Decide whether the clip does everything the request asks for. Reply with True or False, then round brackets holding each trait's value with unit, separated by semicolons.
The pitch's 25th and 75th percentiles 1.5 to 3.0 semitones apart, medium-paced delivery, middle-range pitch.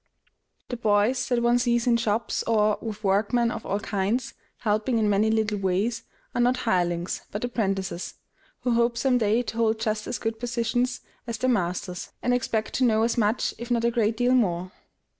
False (2.5 semitones; 190 wpm; 225 Hz)